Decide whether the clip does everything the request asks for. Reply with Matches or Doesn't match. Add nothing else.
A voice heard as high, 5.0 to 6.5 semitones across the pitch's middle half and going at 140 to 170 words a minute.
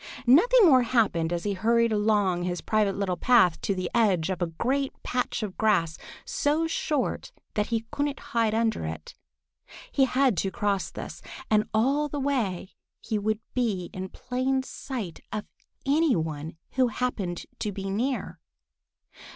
Matches